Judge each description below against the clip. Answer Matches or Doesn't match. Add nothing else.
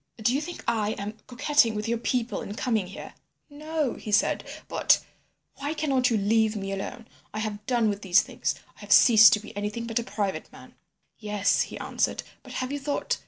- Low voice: Doesn't match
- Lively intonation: Doesn't match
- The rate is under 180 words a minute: Doesn't match